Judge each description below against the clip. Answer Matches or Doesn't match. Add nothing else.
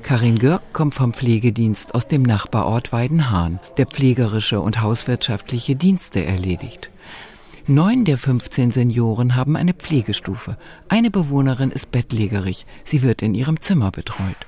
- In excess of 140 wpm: Doesn't match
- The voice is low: Matches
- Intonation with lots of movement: Doesn't match